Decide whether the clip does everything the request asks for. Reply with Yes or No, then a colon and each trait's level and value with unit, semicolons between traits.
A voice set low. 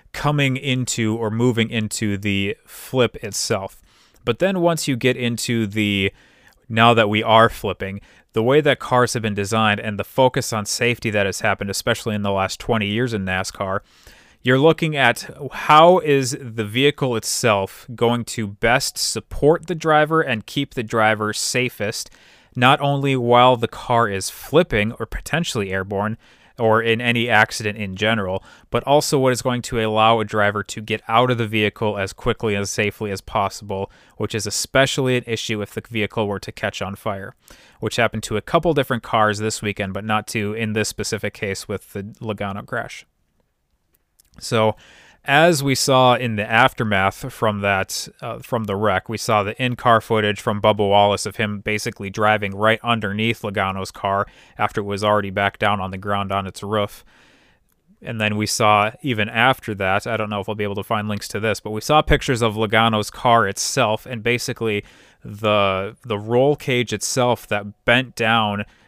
Yes: low, 110 Hz